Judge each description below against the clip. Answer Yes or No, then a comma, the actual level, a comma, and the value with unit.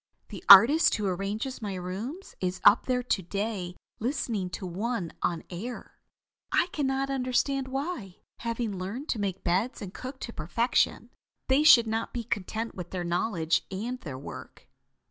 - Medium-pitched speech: No, high, 220 Hz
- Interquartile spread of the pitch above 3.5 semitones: Yes, wide, 5.4 semitones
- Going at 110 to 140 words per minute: No, average, 165 wpm